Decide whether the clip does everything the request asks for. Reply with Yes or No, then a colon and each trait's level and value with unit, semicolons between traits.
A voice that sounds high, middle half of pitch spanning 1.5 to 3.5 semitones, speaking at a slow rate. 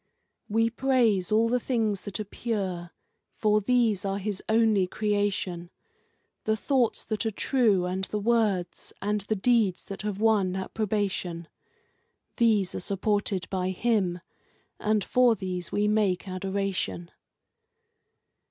Yes: high, 205 Hz; average, 2.8 semitones; slow, 130 wpm